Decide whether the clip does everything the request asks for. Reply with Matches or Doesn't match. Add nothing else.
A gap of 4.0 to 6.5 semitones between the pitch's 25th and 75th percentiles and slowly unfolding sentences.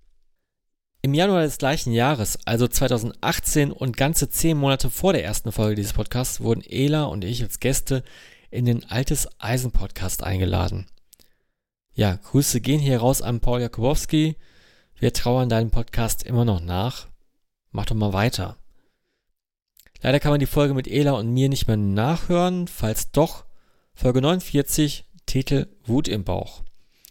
Doesn't match